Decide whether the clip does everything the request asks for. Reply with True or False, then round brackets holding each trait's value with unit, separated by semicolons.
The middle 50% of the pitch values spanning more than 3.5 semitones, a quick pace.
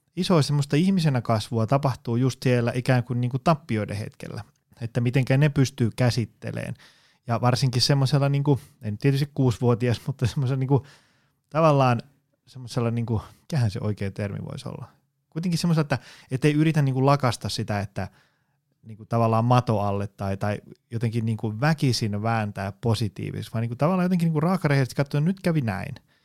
True (3.9 semitones; 165 wpm)